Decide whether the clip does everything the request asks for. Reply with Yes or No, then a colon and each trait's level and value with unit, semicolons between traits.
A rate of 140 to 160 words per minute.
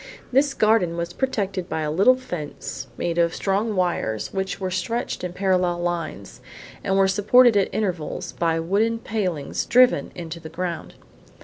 Yes: average, 155 wpm